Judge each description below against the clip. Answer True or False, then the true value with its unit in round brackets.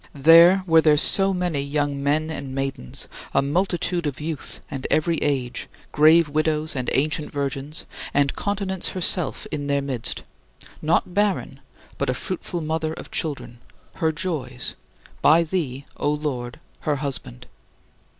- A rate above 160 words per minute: False (140 wpm)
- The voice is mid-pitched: True (150 Hz)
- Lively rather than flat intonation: False (3.2 semitones)